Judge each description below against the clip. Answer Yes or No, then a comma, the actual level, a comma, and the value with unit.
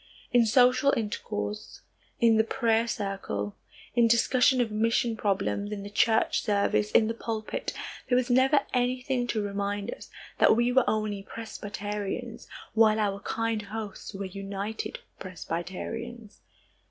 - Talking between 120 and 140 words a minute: Yes, slow, 135 wpm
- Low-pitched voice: No, high, 220 Hz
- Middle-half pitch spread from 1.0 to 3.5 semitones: Yes, average, 2.9 semitones